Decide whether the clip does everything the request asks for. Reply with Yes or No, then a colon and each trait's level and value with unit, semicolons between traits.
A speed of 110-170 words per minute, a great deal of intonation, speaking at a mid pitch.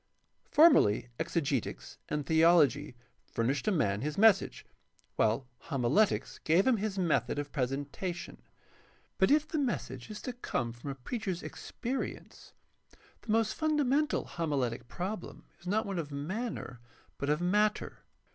Yes: slow, 135 wpm; wide, 7.7 semitones; medium, 170 Hz